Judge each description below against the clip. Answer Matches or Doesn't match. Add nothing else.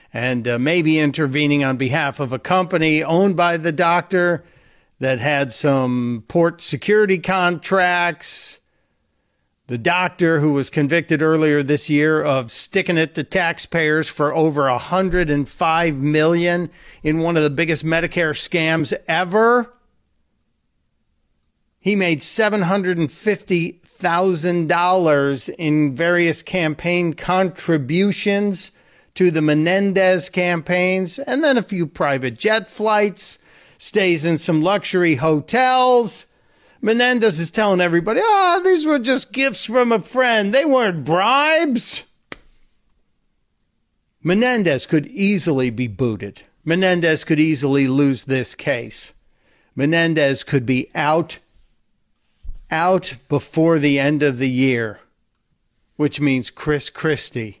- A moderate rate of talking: Doesn't match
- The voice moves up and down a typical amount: Matches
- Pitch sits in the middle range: Matches